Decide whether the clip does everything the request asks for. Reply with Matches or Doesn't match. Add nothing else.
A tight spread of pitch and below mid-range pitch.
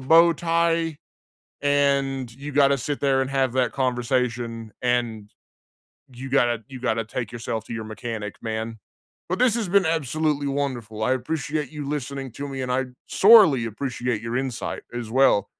Doesn't match